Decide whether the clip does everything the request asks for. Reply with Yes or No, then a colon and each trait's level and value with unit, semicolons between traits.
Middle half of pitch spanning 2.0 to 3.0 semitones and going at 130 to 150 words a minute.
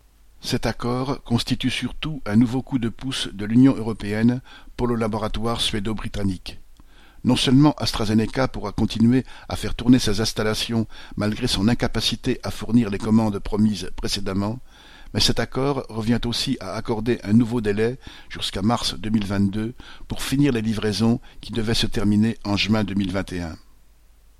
Yes: narrow, 2.6 semitones; slow, 145 wpm